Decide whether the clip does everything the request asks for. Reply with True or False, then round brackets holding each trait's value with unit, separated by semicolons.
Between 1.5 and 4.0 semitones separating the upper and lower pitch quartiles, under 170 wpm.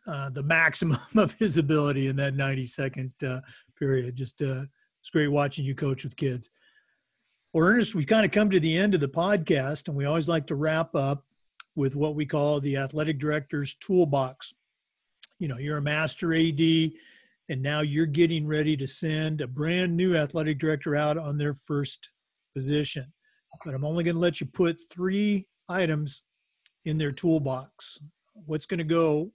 False (2.8 semitones; 180 wpm)